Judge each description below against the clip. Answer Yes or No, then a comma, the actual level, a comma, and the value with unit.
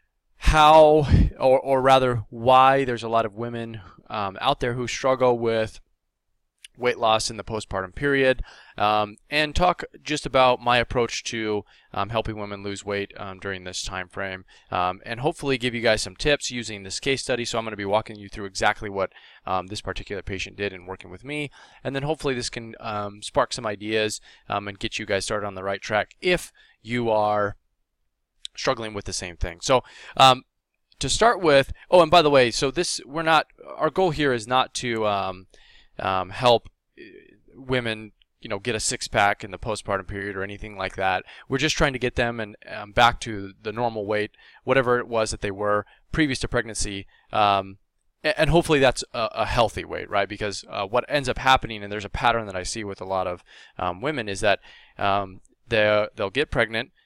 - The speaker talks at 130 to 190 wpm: No, average, 200 wpm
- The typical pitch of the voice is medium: No, low, 110 Hz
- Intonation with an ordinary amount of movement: Yes, average, 4.3 semitones